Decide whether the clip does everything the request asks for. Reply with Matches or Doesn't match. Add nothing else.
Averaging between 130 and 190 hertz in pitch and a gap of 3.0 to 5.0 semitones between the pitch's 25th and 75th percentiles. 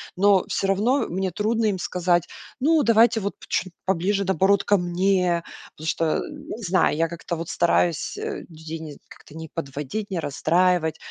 Matches